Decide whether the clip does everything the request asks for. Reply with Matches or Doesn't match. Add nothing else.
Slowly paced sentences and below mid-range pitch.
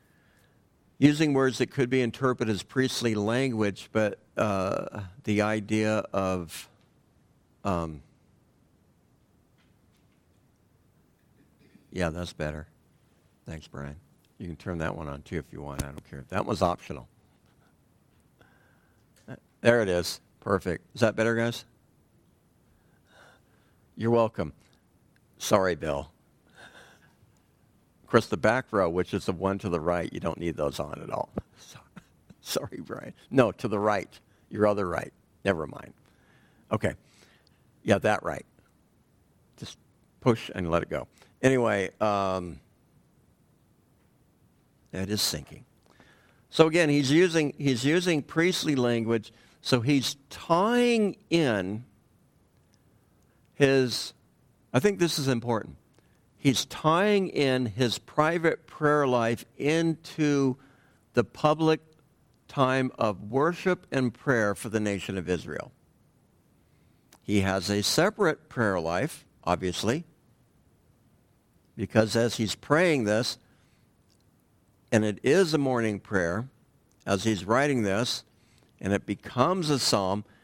Matches